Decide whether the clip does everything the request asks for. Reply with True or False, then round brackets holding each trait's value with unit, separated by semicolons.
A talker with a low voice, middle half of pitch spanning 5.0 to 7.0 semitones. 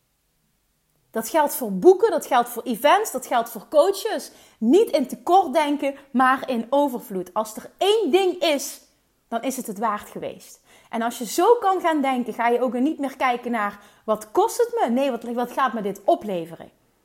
False (260 Hz; 5.4 semitones)